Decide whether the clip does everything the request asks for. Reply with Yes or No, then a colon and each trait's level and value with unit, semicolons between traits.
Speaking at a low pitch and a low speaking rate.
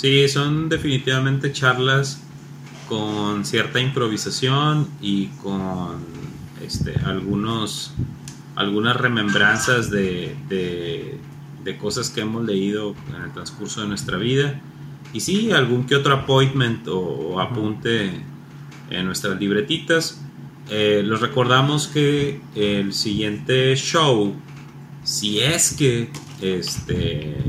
Yes: low, 130 Hz; slow, 105 wpm